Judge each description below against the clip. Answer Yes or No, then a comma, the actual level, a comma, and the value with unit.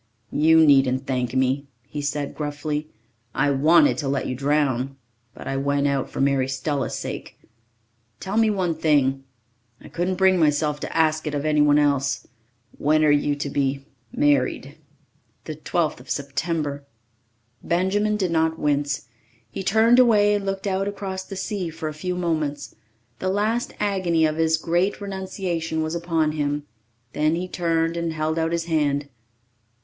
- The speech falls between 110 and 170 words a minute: Yes, average, 160 wpm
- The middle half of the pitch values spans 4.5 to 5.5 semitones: No, average, 3.9 semitones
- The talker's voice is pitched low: No, medium, 155 Hz